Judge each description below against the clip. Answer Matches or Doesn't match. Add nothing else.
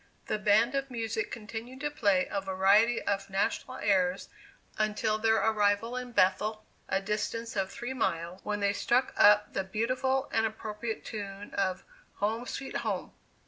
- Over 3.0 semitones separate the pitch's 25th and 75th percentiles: Doesn't match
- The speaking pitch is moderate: Doesn't match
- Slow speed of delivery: Doesn't match